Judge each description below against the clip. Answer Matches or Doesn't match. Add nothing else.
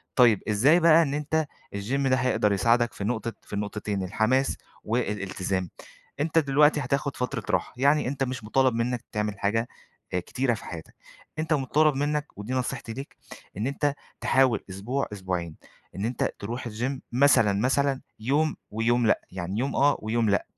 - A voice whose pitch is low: Matches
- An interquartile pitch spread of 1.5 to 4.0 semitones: Doesn't match